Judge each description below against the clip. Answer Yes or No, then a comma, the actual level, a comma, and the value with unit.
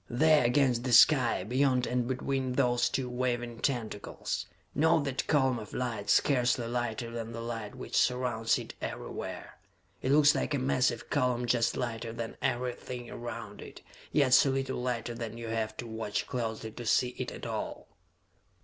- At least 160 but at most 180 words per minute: Yes, average, 165 wpm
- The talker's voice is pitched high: No, low, 120 Hz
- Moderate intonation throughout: No, narrow, 1.9 semitones